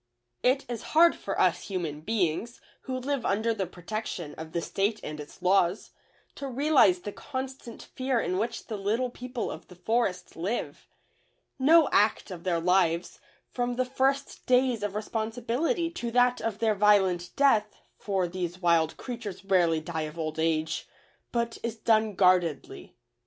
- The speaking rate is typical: Yes, average, 160 wpm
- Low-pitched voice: No, high, 210 Hz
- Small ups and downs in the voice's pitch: No, wide, 5.6 semitones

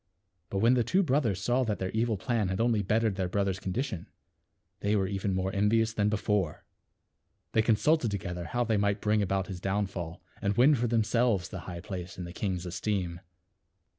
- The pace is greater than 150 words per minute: Yes, average, 195 wpm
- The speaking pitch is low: Yes, low, 100 Hz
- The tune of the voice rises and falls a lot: No, average, 3.2 semitones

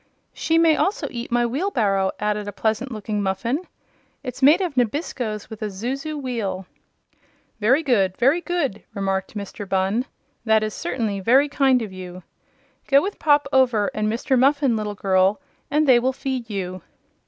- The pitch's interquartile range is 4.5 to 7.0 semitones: Yes, average, 5.1 semitones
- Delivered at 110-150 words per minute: No, average, 165 wpm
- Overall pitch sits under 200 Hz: No, high, 235 Hz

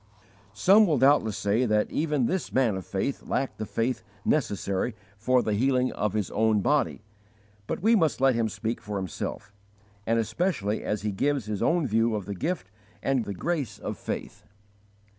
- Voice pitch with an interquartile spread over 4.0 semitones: Yes, average, 4.8 semitones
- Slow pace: No, average, 180 wpm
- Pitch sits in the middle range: No, low, 115 Hz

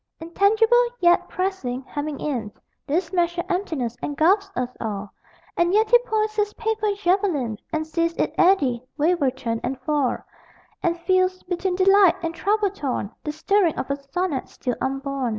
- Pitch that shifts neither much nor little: No, wide, 6.3 semitones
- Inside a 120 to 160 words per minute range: Yes, average, 155 wpm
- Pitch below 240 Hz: No, very high, 340 Hz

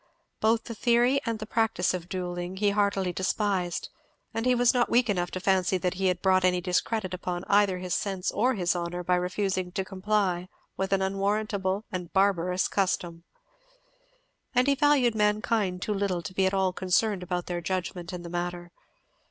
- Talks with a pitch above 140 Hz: Yes, high, 190 Hz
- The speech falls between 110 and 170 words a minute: No, average, 185 wpm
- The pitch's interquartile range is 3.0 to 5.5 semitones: No, narrow, 2.6 semitones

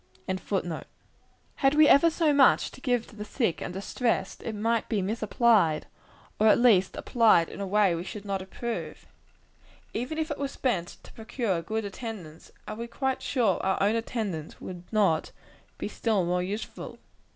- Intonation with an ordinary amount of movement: Yes, average, 4.2 semitones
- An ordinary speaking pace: Yes, average, 175 wpm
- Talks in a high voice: Yes, high, 215 Hz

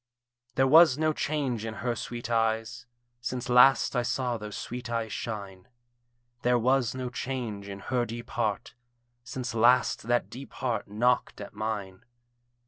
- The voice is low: Yes, low, 120 Hz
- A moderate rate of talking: Yes, average, 150 wpm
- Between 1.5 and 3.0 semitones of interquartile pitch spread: Yes, narrow, 2.4 semitones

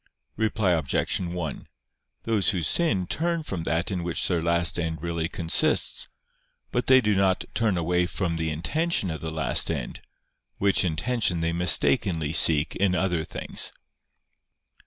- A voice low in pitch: Yes, very low, 90 Hz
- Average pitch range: Yes, average, 3.4 semitones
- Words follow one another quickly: No, average, 150 wpm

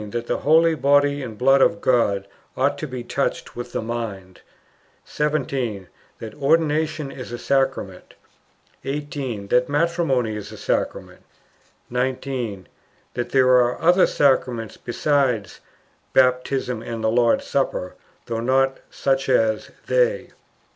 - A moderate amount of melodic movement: Yes, average, 3.5 semitones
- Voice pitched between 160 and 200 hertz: No, low, 130 Hz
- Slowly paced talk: Yes, slow, 130 wpm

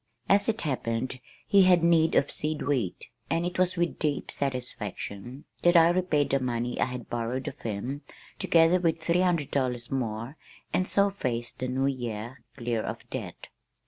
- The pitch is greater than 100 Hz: Yes, low, 135 Hz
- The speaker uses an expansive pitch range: Yes, wide, 5.9 semitones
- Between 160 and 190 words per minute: Yes, average, 175 wpm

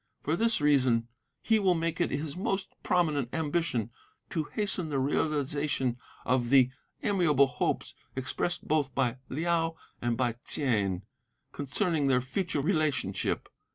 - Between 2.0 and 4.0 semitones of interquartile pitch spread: No, average, 4.7 semitones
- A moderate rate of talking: No, slow, 130 wpm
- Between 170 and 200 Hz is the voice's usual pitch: No, medium, 145 Hz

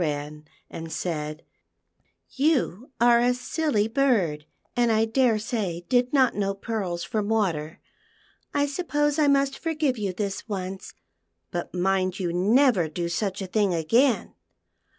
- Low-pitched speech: No, high, 210 Hz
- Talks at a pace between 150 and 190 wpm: No, slow, 135 wpm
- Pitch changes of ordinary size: No, wide, 6.2 semitones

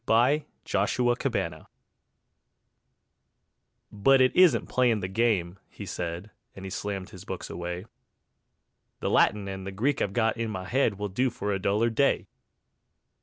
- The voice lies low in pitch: Yes, low, 105 Hz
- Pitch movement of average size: Yes, average, 4.2 semitones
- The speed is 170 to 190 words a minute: No, average, 145 wpm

